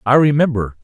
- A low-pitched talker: Yes, low, 130 Hz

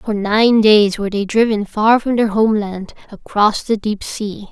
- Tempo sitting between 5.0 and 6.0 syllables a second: No, 4.5 syllables/s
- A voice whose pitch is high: Yes, high, 210 Hz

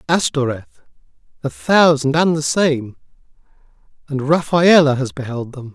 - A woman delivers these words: No, male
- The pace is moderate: No, slow, 105 wpm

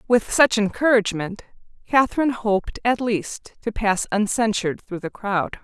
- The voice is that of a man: No, female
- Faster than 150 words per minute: No, average, 140 wpm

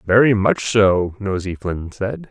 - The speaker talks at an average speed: Yes, average, 155 wpm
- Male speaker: Yes, male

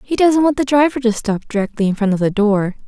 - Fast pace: Yes, fast, 270 wpm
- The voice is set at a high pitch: Yes, high, 235 Hz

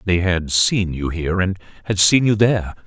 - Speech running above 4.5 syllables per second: Yes, 5.1 syllables/s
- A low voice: Yes, very low, 95 Hz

